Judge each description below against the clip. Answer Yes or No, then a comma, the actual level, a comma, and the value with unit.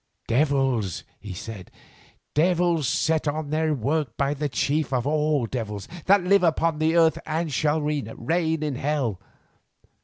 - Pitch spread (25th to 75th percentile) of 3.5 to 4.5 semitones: Yes, average, 3.8 semitones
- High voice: No, medium, 150 Hz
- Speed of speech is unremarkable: Yes, average, 145 wpm